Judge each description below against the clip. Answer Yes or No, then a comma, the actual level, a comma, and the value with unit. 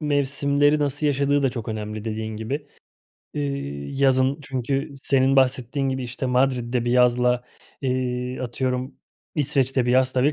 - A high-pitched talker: No, low, 130 Hz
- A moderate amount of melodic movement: No, narrow, 2.1 semitones